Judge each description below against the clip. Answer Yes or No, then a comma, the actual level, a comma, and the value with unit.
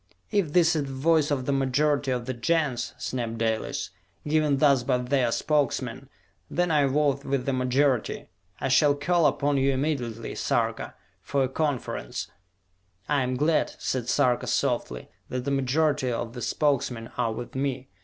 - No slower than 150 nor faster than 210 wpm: Yes, average, 165 wpm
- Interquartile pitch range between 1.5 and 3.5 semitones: Yes, average, 2.8 semitones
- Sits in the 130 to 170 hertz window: Yes, low, 135 Hz